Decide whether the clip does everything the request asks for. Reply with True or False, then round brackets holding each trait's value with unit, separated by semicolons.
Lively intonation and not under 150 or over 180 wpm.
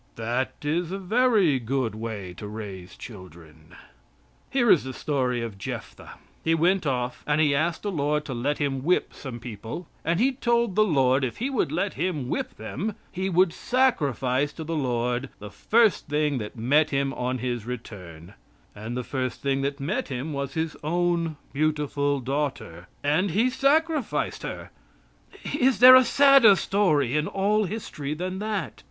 True (7.1 semitones; 170 wpm)